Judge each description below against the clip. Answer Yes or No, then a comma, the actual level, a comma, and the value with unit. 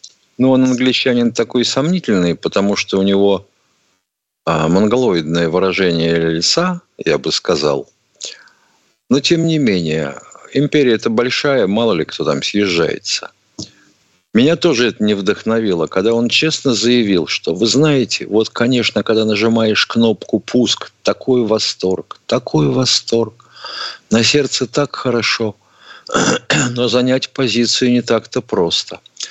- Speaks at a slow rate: No, average, 125 wpm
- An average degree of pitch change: Yes, average, 4.4 semitones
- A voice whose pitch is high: No, low, 115 Hz